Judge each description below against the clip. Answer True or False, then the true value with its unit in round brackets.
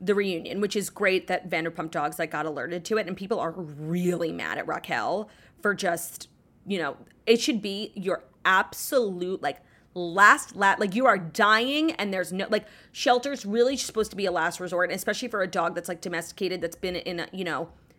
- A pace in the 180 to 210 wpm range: True (205 wpm)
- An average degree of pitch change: True (3.1 semitones)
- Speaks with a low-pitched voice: False (185 Hz)